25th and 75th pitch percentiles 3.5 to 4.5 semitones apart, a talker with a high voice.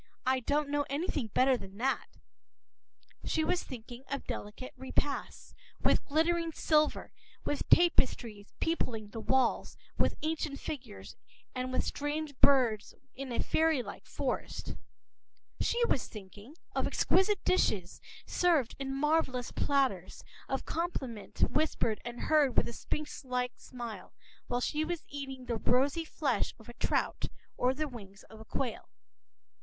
Yes: average, 4.2 semitones; very high, 265 Hz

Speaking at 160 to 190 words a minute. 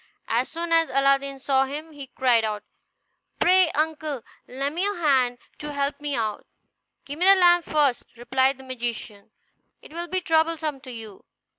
Yes: average, 170 wpm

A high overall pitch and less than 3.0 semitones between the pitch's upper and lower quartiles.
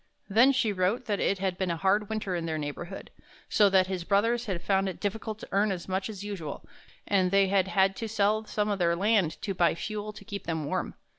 Yes: high, 195 Hz; narrow, 2.4 semitones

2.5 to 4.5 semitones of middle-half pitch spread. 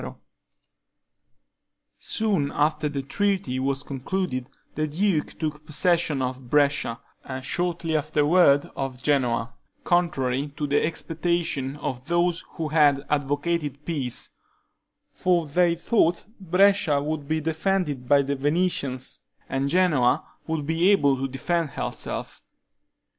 Yes: average, 3.7 semitones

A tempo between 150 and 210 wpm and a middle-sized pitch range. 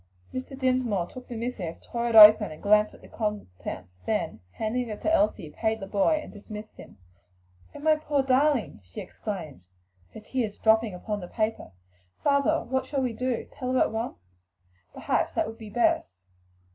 Yes: average, 180 wpm; average, 3.8 semitones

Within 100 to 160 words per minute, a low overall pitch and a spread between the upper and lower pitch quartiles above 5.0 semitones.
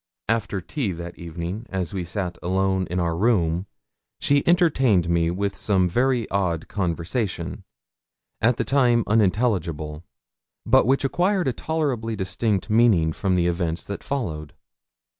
Yes: average, 140 wpm; very low, 95 Hz; wide, 5.4 semitones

